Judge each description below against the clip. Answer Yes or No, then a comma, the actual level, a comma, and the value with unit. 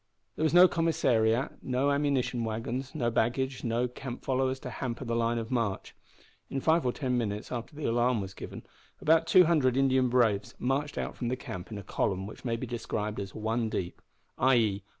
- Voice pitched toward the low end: Yes, low, 125 Hz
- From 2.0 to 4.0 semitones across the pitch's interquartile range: Yes, average, 3.0 semitones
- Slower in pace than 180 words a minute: No, average, 195 wpm